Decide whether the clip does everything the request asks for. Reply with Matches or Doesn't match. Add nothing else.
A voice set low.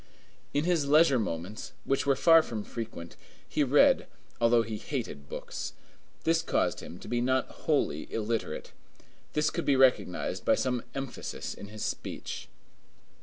Matches